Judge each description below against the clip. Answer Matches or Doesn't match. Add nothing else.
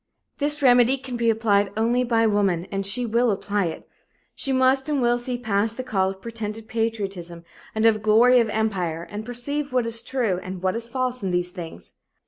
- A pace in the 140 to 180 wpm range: Doesn't match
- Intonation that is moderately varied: Matches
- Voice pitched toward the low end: Doesn't match